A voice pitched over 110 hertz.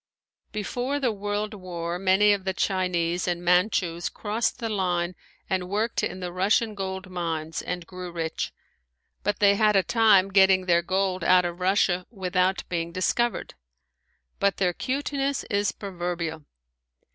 Yes: medium, 185 Hz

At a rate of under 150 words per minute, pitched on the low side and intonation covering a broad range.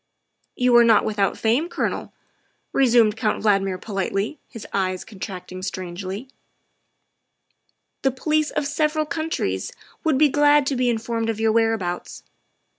No: average, 140 wpm; high, 225 Hz; wide, 5.7 semitones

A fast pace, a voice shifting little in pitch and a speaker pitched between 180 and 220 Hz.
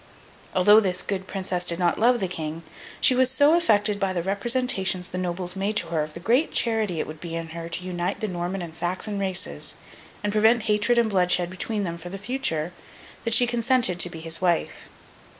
No: fast, 210 wpm; average, 4.0 semitones; high, 190 Hz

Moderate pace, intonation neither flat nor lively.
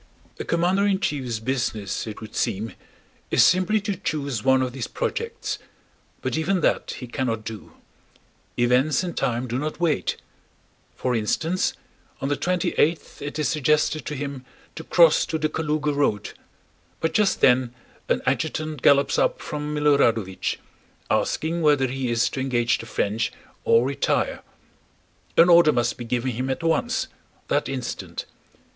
Yes: average, 155 wpm; average, 4.8 semitones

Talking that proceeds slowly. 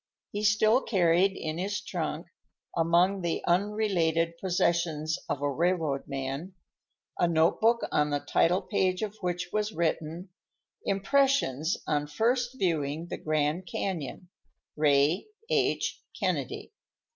Yes: slow, 120 wpm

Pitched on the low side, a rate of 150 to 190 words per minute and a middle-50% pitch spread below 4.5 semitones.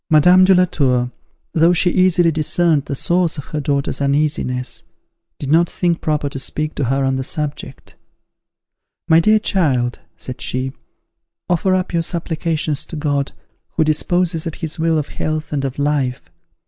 No: medium, 155 Hz; average, 165 wpm; average, 3.4 semitones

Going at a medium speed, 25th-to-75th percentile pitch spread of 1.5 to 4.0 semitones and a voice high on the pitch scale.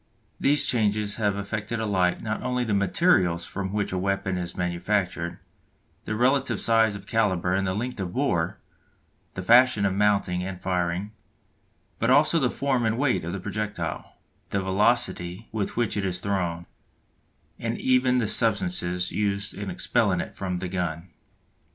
No: average, 155 wpm; average, 3.7 semitones; low, 100 Hz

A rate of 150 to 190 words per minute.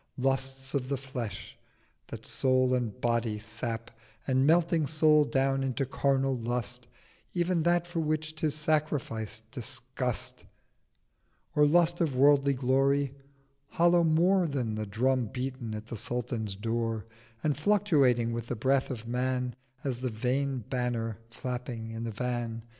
No: average, 140 wpm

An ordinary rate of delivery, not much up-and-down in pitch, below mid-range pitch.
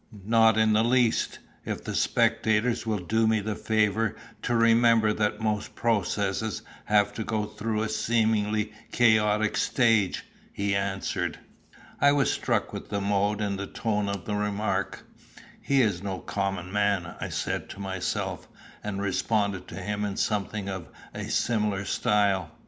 Yes: average, 150 wpm; narrow, 1.8 semitones; low, 105 Hz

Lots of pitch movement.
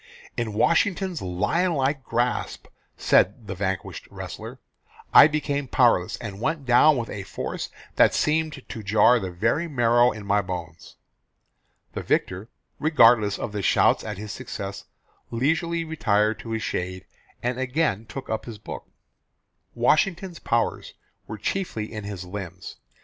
Yes: wide, 6.2 semitones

